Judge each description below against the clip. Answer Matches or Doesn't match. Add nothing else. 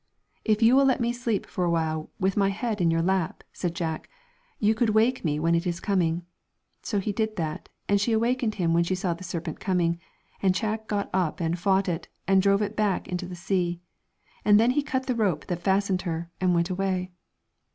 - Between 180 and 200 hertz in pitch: Matches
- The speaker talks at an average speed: Doesn't match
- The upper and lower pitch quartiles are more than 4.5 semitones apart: Doesn't match